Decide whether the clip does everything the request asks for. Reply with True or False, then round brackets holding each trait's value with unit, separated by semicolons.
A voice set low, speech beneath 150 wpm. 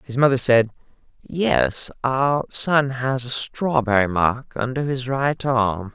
True (125 Hz; 140 wpm)